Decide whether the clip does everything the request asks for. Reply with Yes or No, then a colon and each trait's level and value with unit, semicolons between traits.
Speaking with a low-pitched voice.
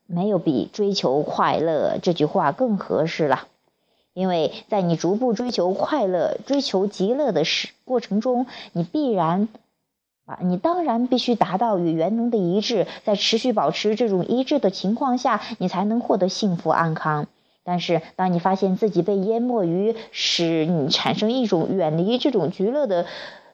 No: high, 205 Hz